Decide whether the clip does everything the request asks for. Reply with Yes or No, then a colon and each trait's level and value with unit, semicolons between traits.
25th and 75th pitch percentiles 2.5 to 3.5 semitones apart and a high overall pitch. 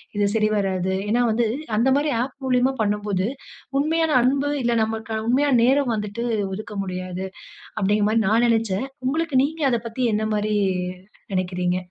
No: average, 4.0 semitones; high, 225 Hz